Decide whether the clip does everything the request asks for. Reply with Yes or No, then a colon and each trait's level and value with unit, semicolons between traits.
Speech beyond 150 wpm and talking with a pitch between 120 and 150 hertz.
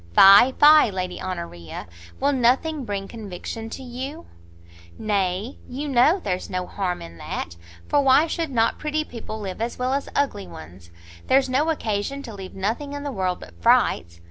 No: average, 170 wpm; high, 230 Hz